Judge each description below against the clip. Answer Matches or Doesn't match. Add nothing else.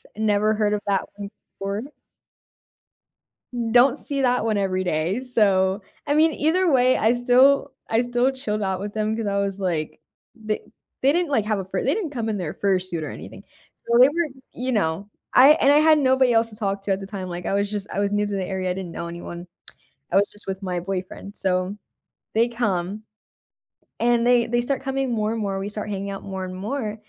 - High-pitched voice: Matches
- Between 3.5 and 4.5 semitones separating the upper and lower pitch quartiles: Matches